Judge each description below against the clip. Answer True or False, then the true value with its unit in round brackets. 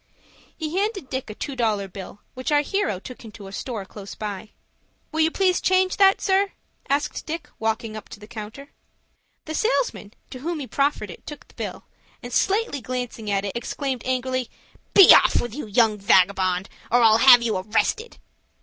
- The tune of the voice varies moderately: False (6.5 semitones)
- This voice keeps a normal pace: True (180 wpm)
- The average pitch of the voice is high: True (250 Hz)